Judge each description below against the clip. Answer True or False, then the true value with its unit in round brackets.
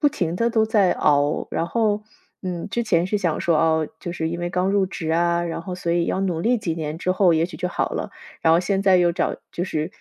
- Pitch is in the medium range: True (175 Hz)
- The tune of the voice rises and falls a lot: False (2.8 semitones)